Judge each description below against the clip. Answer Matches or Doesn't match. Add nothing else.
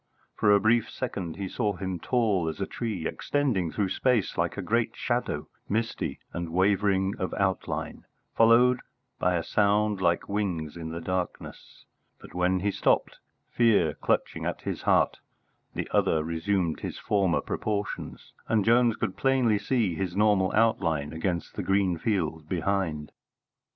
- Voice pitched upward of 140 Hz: Doesn't match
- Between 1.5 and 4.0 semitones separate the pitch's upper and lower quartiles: Matches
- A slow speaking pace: Doesn't match